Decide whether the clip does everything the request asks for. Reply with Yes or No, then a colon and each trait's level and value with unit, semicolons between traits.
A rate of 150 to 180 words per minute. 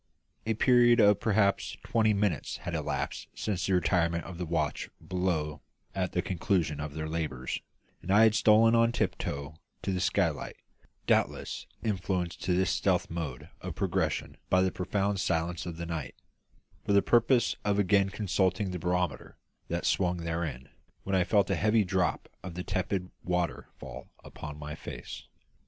Yes: average, 160 wpm